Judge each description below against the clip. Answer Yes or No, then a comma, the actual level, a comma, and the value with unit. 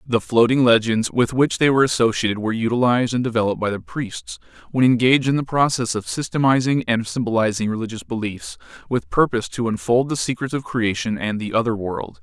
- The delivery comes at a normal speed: Yes, average, 180 wpm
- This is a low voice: Yes, low, 120 Hz